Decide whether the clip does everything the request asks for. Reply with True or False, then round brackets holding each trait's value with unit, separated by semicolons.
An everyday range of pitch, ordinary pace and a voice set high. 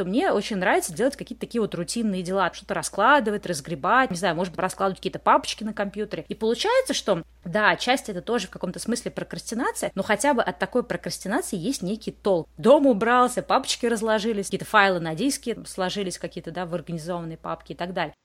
False (4.4 semitones; 195 wpm; 200 Hz)